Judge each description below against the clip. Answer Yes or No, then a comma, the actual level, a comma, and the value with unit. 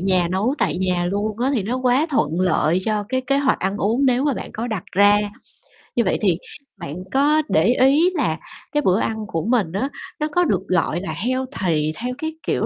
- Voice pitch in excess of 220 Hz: No, high, 215 Hz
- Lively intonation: Yes, wide, 5.9 semitones